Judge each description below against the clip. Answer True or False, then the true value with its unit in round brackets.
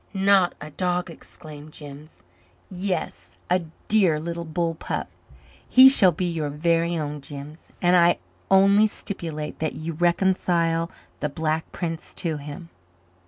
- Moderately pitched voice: True (165 Hz)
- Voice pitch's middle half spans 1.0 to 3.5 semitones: True (2.8 semitones)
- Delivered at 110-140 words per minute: True (135 wpm)